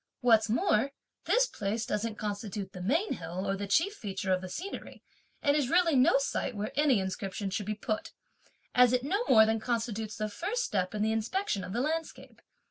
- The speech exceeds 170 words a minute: Yes, average, 200 wpm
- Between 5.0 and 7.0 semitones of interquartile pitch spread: Yes, wide, 5.5 semitones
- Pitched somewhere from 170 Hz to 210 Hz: No, high, 220 Hz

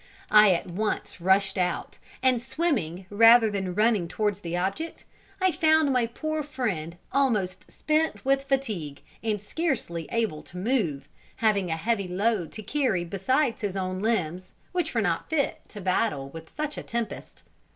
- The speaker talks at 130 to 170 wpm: Yes, average, 160 wpm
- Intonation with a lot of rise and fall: Yes, wide, 6.3 semitones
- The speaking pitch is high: Yes, high, 210 Hz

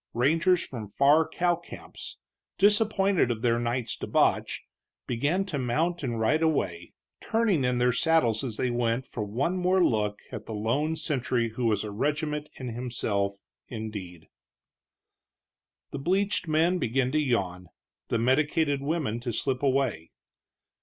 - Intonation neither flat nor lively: No, wide, 5.8 semitones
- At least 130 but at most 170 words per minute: Yes, average, 145 wpm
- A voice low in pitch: Yes, low, 130 Hz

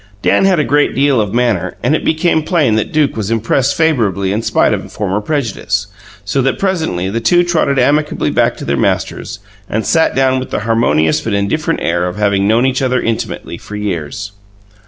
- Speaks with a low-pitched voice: Yes, low, 115 Hz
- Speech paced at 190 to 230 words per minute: Yes, average, 200 wpm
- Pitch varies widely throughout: Yes, wide, 6.2 semitones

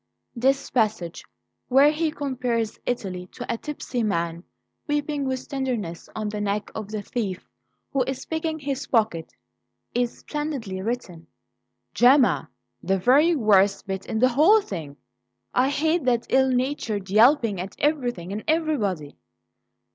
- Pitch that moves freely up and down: Yes, wide, 5.8 semitones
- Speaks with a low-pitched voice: No, high, 240 Hz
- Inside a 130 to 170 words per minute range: Yes, average, 140 wpm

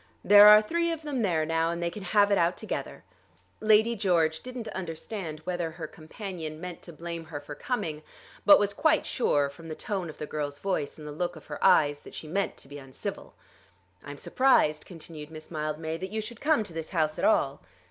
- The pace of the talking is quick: Yes, fast, 220 wpm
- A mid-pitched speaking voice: Yes, medium, 170 Hz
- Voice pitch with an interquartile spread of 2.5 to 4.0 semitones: No, average, 4.8 semitones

